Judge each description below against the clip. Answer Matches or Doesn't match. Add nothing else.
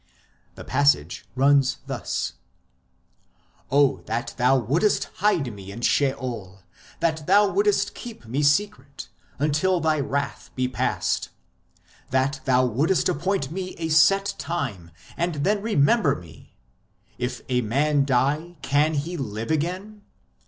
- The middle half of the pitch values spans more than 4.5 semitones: Matches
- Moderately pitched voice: Matches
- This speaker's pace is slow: Matches